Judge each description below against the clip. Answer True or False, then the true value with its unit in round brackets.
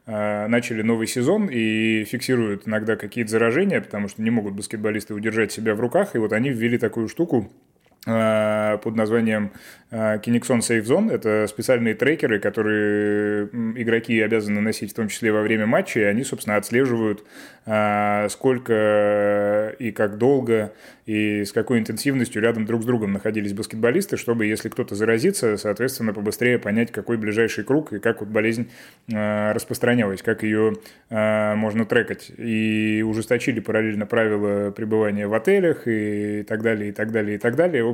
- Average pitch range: False (1.7 semitones)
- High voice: False (110 Hz)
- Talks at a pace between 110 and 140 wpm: False (150 wpm)